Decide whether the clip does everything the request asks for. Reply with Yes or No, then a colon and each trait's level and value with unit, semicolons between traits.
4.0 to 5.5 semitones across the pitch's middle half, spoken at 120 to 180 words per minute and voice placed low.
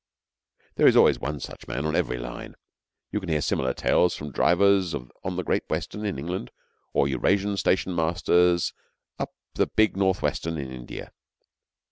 Yes: average, 5.2 semitones; average, 160 wpm; very low, 85 Hz